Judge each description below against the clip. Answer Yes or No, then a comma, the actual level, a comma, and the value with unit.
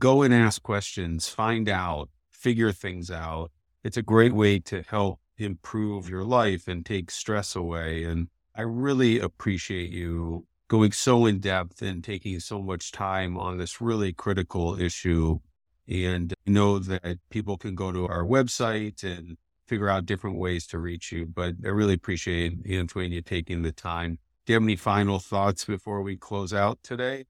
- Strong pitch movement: No, average, 3.5 semitones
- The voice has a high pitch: No, very low, 95 Hz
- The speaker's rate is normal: Yes, average, 175 wpm